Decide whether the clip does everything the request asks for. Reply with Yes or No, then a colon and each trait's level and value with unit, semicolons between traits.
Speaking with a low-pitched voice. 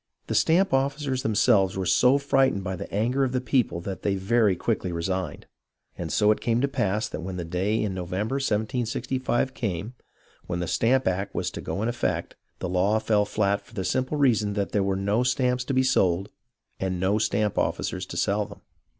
Yes: low, 105 Hz